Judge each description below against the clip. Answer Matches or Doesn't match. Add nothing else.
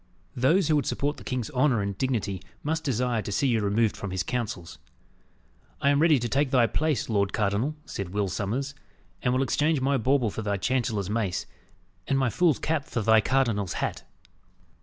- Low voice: Matches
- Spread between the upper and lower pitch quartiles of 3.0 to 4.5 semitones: Doesn't match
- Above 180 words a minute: Matches